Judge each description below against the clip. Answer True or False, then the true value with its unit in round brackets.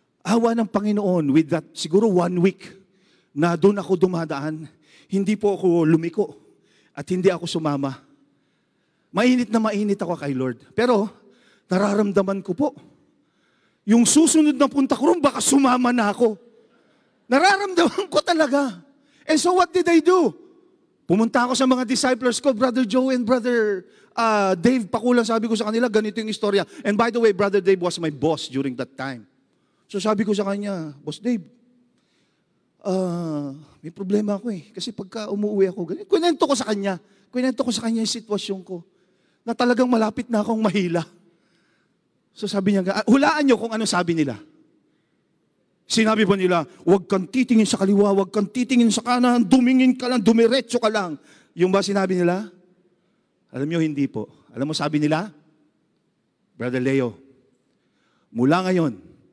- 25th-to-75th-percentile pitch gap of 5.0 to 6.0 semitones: True (5.4 semitones)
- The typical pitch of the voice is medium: False (210 Hz)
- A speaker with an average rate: True (160 wpm)